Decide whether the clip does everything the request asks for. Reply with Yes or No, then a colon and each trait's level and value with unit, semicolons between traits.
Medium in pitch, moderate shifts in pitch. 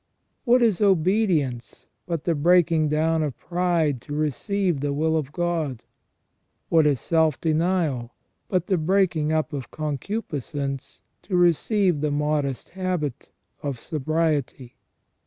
Yes: medium, 155 Hz; average, 3.5 semitones